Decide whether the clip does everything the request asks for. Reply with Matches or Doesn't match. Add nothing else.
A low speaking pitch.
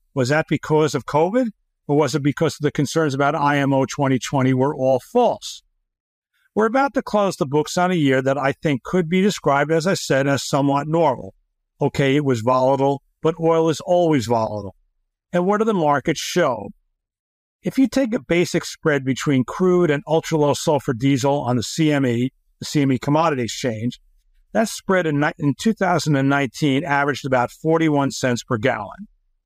Doesn't match